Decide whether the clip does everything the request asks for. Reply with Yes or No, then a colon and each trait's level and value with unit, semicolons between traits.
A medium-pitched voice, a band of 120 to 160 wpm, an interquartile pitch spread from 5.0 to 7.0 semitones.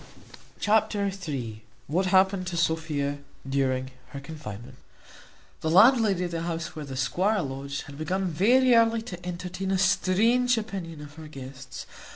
Yes: medium, 170 Hz; average, 150 wpm; wide, 5.5 semitones